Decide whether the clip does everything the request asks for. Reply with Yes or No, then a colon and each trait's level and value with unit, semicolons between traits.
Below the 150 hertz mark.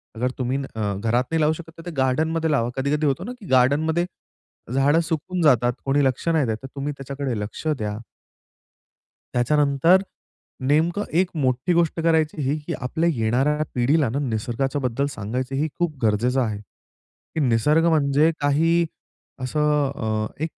Yes: medium, 140 Hz